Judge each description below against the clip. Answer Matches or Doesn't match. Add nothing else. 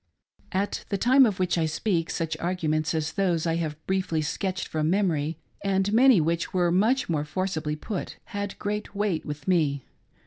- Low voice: Doesn't match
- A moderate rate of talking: Matches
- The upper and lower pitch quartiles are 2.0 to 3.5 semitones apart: Doesn't match